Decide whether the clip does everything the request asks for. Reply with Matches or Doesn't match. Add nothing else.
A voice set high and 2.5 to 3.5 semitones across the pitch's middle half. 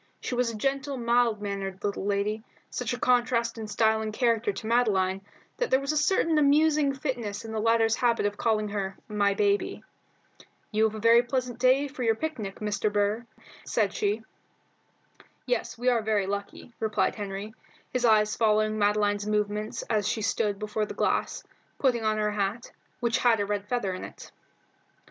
Matches